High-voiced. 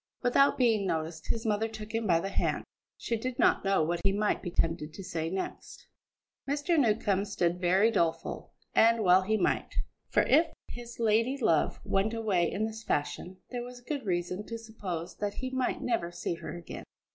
Yes: high, 210 Hz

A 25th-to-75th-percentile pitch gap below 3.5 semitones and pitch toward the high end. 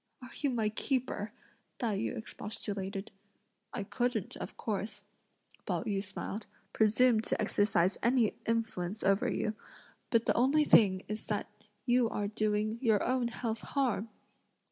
Yes: average, 2.7 semitones; high, 220 Hz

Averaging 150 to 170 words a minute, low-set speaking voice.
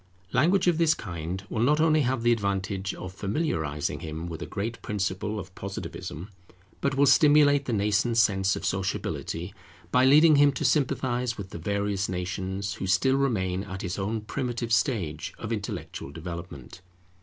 Yes: average, 165 wpm; low, 100 Hz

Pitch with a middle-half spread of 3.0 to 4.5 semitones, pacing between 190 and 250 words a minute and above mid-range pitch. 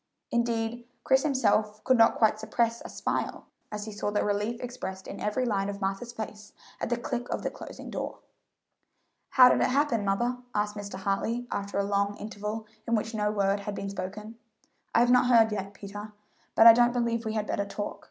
No: narrow, 2.6 semitones; average, 200 wpm; high, 215 Hz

